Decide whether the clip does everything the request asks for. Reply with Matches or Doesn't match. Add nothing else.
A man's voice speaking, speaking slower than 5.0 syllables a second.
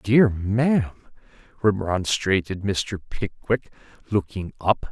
Matches